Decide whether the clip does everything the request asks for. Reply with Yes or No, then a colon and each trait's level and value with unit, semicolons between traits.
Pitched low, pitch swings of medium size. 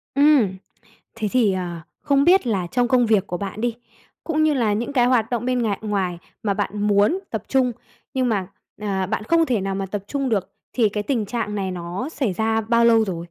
No: high, 220 Hz; average, 4.1 semitones